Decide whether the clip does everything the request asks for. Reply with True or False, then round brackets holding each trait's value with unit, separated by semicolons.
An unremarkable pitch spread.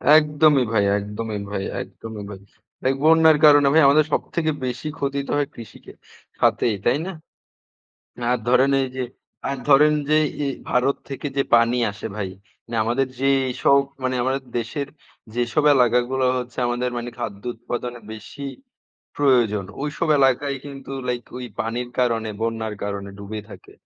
True (3.5 semitones)